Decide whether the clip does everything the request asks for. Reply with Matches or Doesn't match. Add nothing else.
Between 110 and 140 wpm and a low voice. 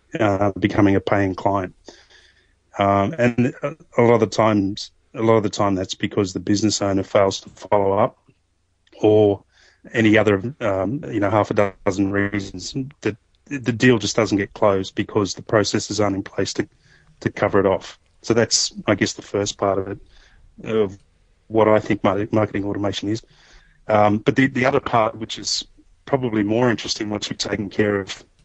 Doesn't match